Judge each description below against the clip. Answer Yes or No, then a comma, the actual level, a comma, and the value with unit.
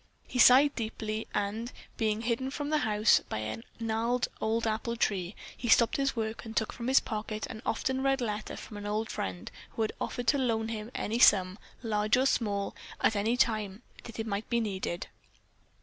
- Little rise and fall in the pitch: Yes, narrow, 2.2 semitones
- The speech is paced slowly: No, average, 195 wpm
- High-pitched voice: Yes, high, 220 Hz